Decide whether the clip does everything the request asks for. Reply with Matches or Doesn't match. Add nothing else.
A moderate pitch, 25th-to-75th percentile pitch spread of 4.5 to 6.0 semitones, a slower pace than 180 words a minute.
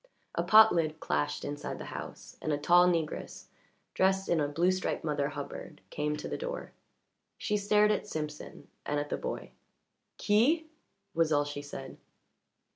Matches